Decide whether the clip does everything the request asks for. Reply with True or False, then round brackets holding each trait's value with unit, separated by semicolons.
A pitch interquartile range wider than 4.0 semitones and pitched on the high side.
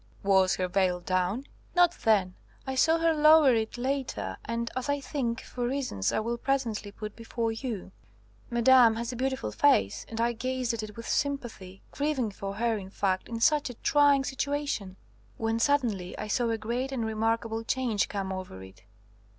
True (4.4 semitones; 230 Hz)